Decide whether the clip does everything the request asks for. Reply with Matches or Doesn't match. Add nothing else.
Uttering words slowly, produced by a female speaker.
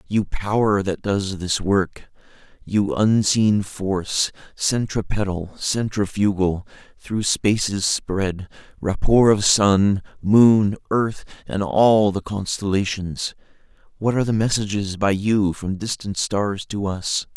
Doesn't match